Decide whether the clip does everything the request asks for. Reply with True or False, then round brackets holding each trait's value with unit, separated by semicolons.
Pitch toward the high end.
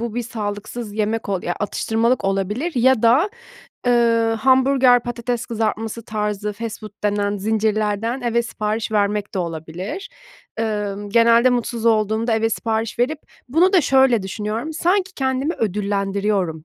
True (225 Hz)